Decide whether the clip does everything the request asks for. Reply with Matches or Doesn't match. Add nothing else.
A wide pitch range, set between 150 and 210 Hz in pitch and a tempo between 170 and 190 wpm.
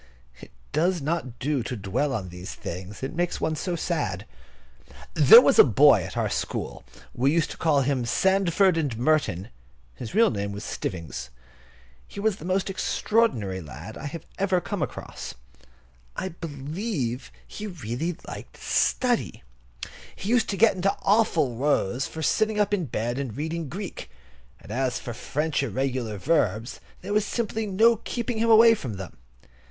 Doesn't match